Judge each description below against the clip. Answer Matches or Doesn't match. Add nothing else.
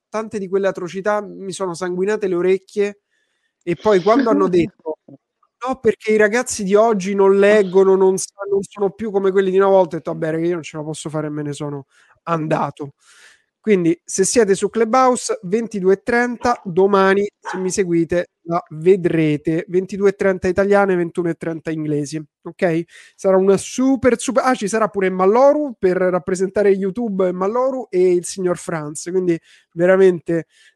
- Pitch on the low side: Doesn't match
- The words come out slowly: Doesn't match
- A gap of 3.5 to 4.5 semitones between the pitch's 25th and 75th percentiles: Doesn't match